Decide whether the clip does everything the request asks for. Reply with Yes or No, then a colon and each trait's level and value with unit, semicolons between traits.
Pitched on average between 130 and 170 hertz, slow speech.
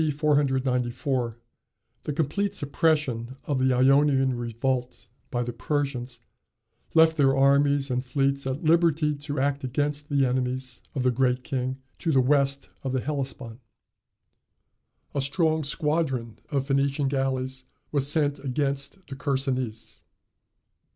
Yes: low, 135 Hz; slow, 125 wpm